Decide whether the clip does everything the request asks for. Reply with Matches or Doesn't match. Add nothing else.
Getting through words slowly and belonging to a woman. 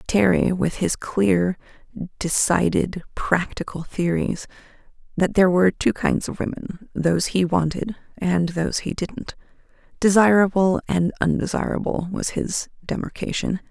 Matches